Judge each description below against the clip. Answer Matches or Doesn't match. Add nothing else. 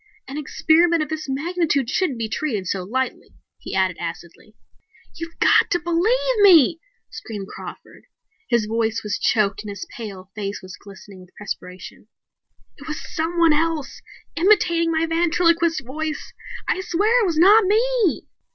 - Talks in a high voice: Matches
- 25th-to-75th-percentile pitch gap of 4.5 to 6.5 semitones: Doesn't match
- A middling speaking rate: Matches